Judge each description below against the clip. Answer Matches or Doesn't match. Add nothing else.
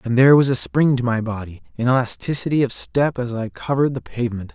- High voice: Doesn't match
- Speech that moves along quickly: Matches